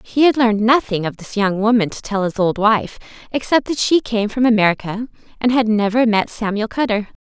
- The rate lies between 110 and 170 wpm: No, fast, 205 wpm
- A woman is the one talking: Yes, female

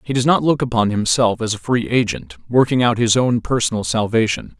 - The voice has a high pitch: No, low, 115 Hz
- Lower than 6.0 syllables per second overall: Yes, 5.5 syllables/s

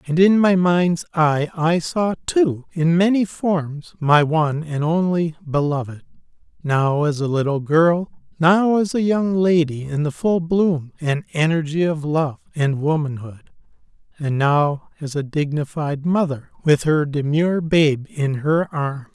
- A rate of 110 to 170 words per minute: Yes, average, 155 wpm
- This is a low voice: No, medium, 160 Hz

